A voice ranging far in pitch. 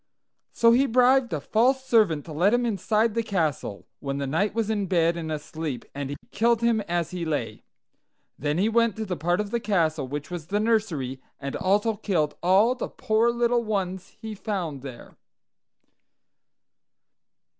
Yes: wide, 6.2 semitones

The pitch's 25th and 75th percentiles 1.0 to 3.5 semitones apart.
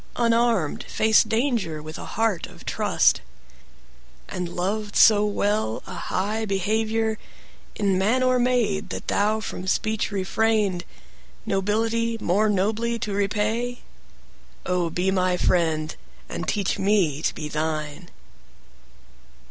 No: average, 4.0 semitones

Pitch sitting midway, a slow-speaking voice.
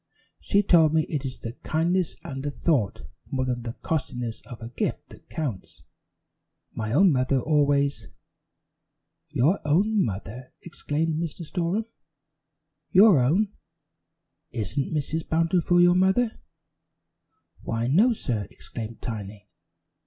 Yes: medium, 150 Hz; slow, 125 wpm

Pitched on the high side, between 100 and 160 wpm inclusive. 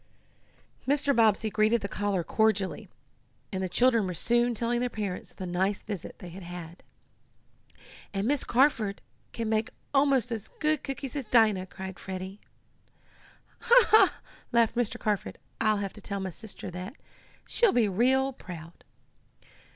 Yes: high, 215 Hz; average, 150 wpm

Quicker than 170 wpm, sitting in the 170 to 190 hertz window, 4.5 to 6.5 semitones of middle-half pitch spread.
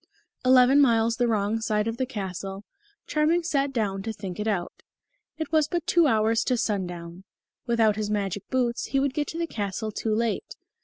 No: average, 190 wpm; high, 225 Hz; average, 4.8 semitones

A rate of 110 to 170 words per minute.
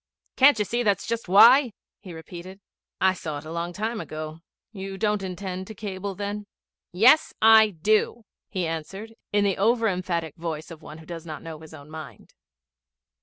No: average, 180 wpm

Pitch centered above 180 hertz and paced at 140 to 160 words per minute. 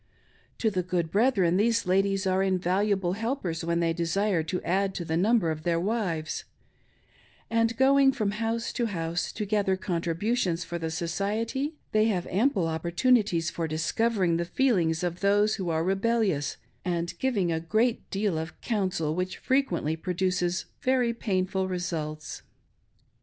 Yes: high, 190 Hz; average, 150 wpm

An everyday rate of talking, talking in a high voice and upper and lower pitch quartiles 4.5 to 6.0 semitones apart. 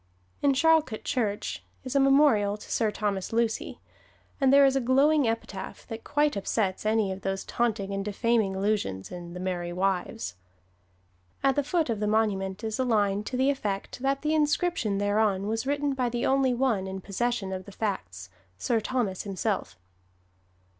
Yes: average, 175 wpm; high, 220 Hz; average, 5.3 semitones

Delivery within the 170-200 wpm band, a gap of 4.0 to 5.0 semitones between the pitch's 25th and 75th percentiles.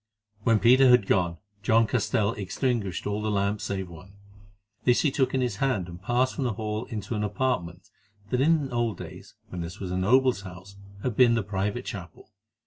Yes: average, 195 wpm; average, 4.4 semitones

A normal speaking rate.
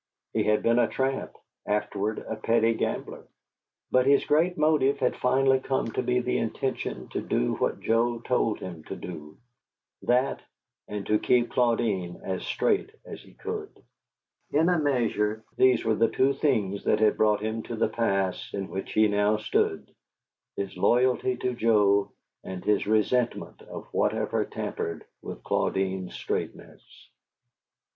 Yes: average, 150 wpm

